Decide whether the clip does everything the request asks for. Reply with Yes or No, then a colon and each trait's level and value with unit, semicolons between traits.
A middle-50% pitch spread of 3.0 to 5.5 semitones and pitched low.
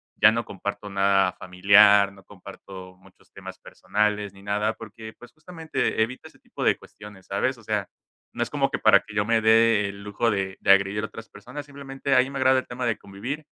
Yes: average, 3.3 semitones; low, 105 Hz